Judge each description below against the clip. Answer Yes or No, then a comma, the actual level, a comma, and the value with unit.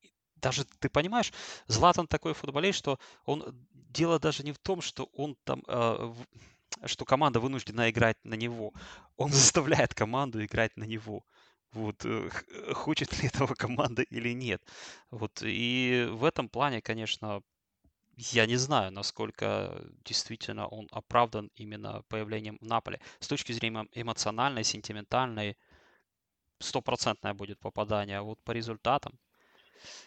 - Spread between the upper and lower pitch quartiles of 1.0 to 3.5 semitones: No, average, 4.1 semitones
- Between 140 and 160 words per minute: No, average, 130 wpm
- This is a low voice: Yes, low, 115 Hz